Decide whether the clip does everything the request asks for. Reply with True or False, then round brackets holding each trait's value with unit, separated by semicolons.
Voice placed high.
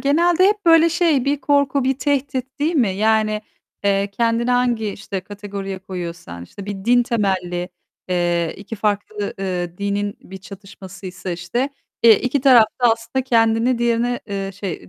True (215 Hz)